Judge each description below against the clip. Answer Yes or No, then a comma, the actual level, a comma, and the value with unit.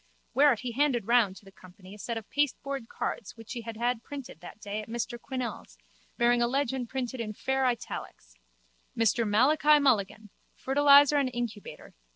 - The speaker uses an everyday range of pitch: Yes, average, 3.7 semitones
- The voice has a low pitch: No, high, 240 Hz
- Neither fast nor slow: Yes, average, 175 wpm